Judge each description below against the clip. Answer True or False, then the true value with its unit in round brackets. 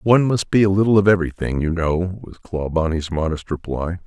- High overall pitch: False (90 Hz)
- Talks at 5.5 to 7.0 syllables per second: True (5.7 syllables/s)